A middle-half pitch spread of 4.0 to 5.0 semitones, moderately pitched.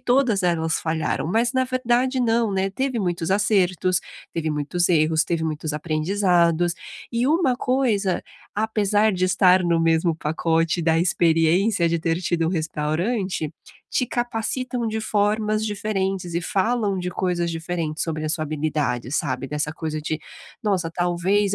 Yes: average, 4.7 semitones; medium, 180 Hz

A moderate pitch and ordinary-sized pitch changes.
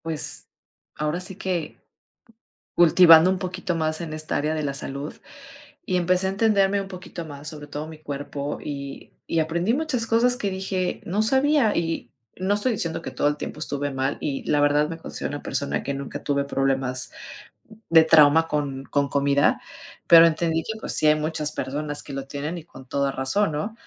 Yes: medium, 155 Hz; average, 4.2 semitones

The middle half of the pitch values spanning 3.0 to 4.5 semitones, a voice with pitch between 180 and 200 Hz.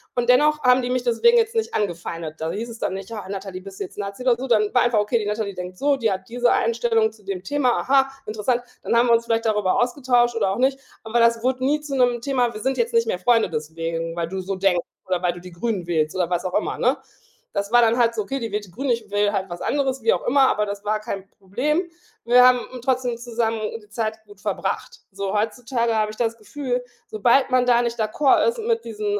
No: average, 3.9 semitones; high, 230 Hz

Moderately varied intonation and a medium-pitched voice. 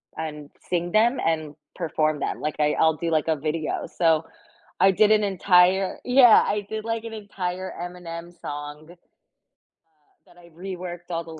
Yes: average, 3.5 semitones; medium, 175 Hz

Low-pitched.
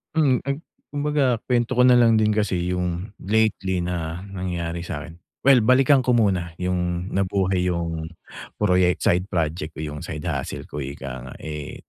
Yes: very low, 90 Hz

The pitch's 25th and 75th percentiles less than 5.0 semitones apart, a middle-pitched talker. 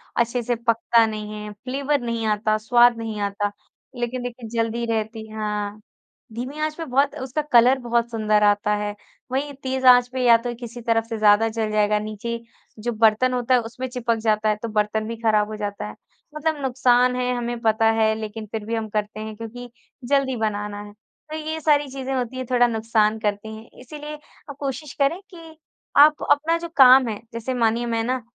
No: average, 2.9 semitones; high, 230 Hz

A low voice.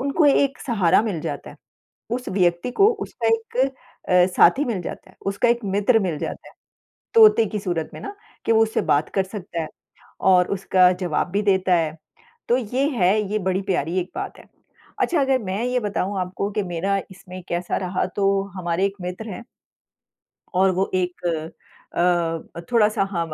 No: high, 195 Hz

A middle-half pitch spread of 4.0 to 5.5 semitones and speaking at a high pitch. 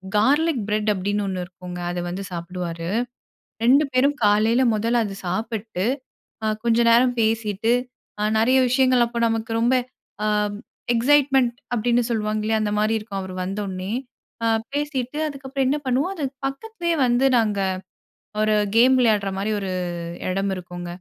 Yes: average, 4.3 semitones; high, 225 Hz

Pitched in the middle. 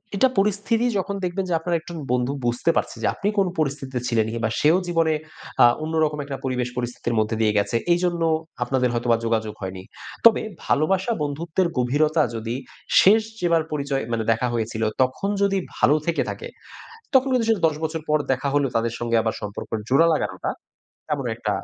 Yes: medium, 145 Hz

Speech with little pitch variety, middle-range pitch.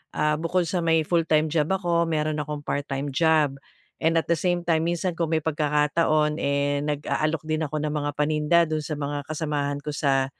Yes: narrow, 2.0 semitones; medium, 155 Hz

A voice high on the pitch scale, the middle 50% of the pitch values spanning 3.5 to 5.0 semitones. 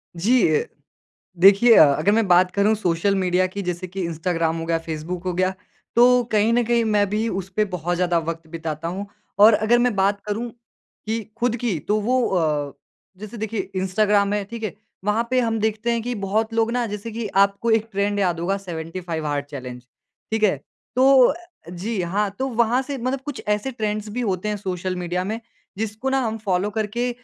Yes: high, 205 Hz; average, 4.0 semitones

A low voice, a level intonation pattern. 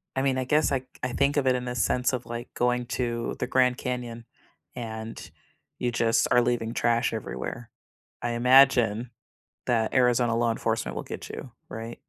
Yes: low, 120 Hz; narrow, 1.6 semitones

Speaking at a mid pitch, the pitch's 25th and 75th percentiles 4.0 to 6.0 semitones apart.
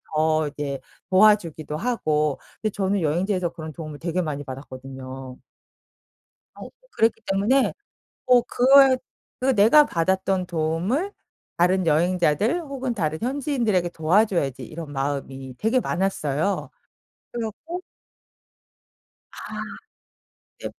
No: medium, 180 Hz; wide, 6.6 semitones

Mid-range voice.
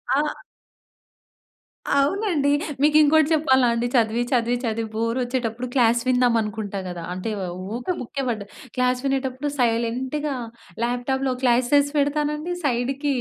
No: very high, 255 Hz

